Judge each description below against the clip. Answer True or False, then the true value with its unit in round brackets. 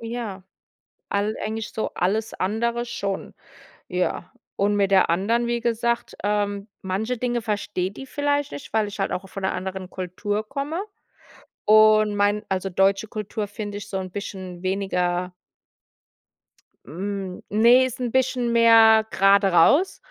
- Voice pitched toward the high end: True (205 Hz)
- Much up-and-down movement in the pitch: False (3.2 semitones)